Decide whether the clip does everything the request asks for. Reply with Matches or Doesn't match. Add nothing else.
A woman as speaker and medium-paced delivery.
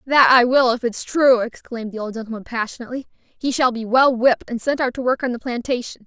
Doesn't match